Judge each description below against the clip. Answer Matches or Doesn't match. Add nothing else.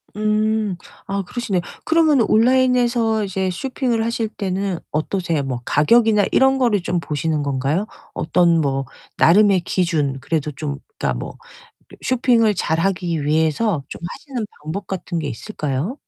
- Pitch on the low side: Doesn't match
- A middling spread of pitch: Doesn't match